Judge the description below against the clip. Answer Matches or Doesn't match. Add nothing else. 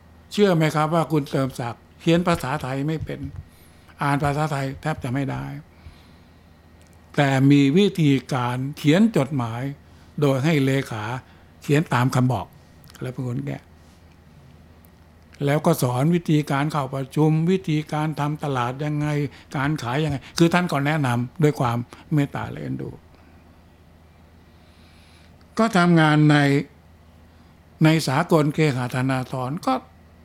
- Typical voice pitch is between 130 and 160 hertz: Matches